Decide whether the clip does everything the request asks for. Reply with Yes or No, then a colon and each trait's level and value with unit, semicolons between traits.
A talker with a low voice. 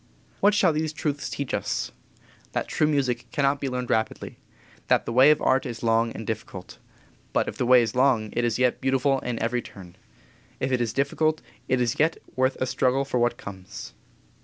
Yes: low, 125 Hz